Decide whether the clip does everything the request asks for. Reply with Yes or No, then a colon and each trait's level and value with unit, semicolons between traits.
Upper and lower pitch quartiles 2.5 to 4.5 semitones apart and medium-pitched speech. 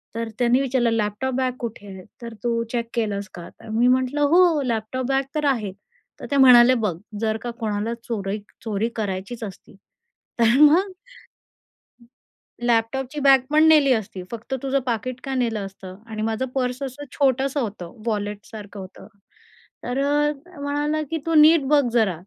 No: average, 4.0 semitones; high, 240 Hz